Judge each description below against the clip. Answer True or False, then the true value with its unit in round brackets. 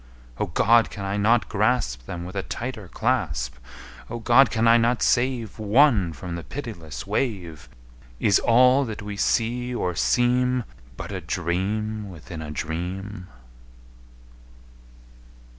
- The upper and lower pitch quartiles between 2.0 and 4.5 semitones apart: False (5.3 semitones)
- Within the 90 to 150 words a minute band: True (135 wpm)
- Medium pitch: False (105 Hz)